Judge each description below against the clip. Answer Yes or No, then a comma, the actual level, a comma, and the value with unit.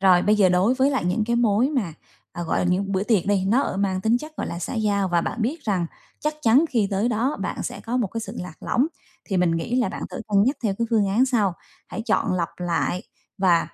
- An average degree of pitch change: Yes, average, 4.3 semitones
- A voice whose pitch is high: Yes, high, 205 Hz